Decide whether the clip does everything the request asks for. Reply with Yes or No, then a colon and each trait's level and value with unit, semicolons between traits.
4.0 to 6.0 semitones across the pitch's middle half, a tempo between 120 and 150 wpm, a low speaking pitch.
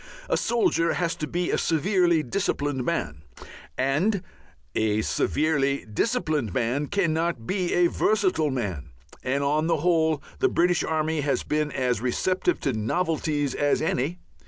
No: average, 4.4 semitones; average, 140 wpm; medium, 155 Hz